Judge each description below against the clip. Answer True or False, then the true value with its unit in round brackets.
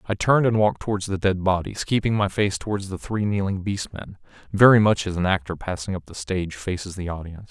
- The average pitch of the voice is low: True (95 Hz)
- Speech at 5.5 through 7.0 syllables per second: True (6.1 syllables/s)